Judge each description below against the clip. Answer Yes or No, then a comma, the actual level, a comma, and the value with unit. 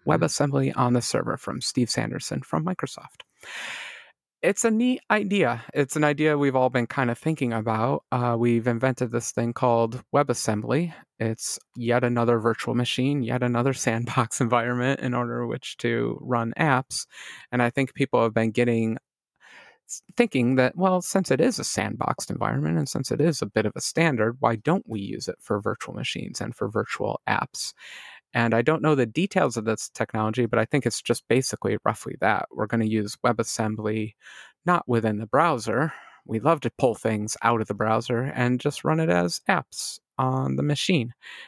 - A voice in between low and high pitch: No, low, 120 Hz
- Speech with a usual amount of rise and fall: Yes, average, 3.4 semitones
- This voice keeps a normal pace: Yes, average, 180 wpm